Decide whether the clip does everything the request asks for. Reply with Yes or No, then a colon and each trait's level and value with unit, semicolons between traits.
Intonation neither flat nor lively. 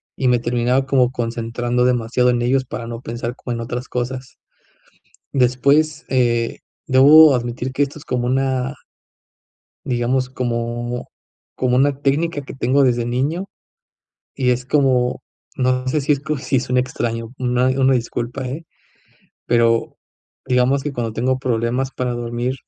No: narrow, 1.9 semitones